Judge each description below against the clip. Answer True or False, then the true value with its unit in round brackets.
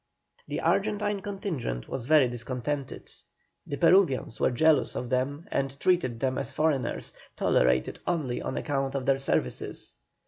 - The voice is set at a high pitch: False (135 Hz)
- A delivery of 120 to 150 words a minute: True (140 wpm)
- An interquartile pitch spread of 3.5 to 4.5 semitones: True (4.2 semitones)